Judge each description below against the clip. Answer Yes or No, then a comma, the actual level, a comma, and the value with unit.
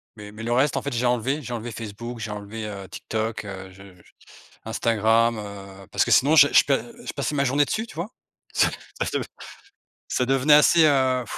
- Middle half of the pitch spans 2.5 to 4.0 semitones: No, average, 4.7 semitones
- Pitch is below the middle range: Yes, low, 120 Hz